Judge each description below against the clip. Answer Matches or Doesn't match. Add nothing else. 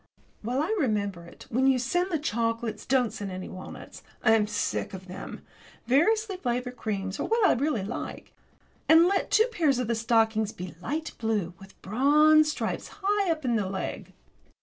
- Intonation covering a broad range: Matches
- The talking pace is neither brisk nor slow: Matches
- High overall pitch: Matches